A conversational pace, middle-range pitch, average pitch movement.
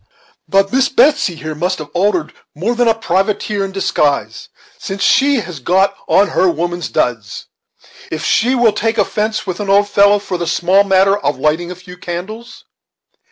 No: average, 175 wpm; high, 195 Hz; average, 3.4 semitones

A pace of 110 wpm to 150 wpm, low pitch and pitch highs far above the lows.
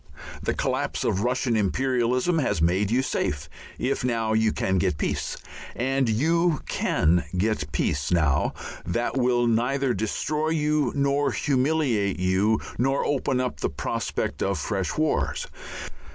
Yes: average, 140 wpm; low, 120 Hz; wide, 5.9 semitones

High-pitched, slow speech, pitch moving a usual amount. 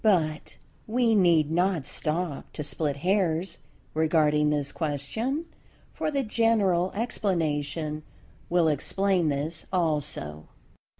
No: medium, 165 Hz; slow, 105 wpm; average, 4.5 semitones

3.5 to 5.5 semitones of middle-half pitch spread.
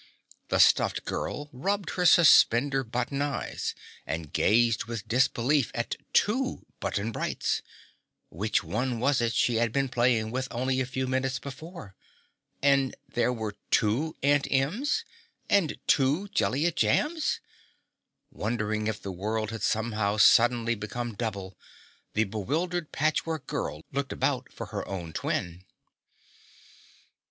Yes: average, 4.6 semitones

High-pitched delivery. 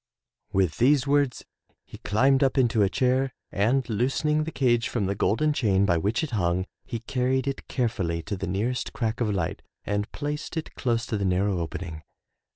No: low, 115 Hz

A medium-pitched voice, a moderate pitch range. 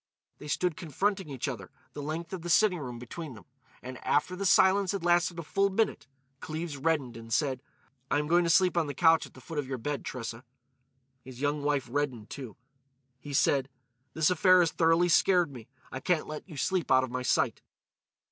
Yes: medium, 150 Hz; average, 4.9 semitones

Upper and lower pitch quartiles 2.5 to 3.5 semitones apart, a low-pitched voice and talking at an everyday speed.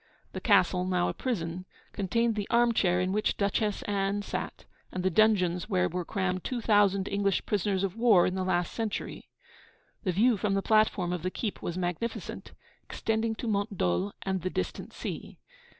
No: average, 3.0 semitones; high, 195 Hz; average, 180 wpm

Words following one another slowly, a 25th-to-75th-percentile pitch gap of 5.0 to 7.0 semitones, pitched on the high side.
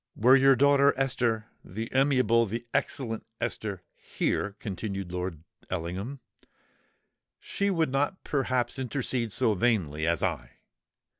No: slow, 115 wpm; wide, 5.5 semitones; low, 115 Hz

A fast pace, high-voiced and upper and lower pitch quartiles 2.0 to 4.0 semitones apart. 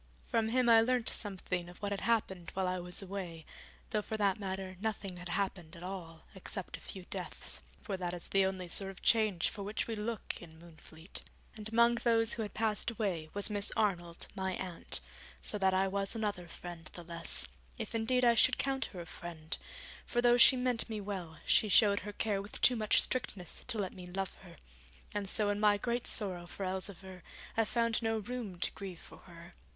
Yes: fast, 210 wpm; high, 200 Hz; average, 3.6 semitones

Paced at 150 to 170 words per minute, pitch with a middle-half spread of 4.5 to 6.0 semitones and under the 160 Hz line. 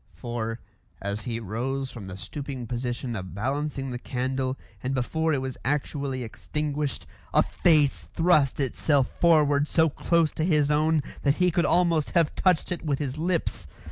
No: average, 165 wpm; average, 3.9 semitones; medium, 140 Hz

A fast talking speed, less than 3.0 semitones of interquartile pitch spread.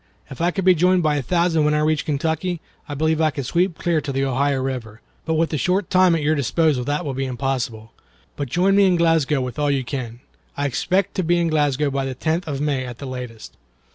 No: fast, 245 wpm; average, 3.9 semitones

